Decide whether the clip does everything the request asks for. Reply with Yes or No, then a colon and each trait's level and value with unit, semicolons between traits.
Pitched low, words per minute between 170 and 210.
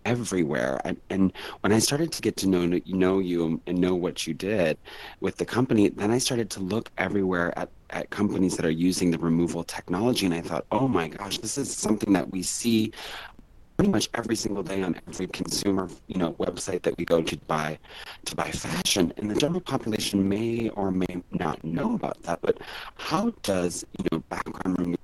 Yes: very low, 95 Hz; average, 200 wpm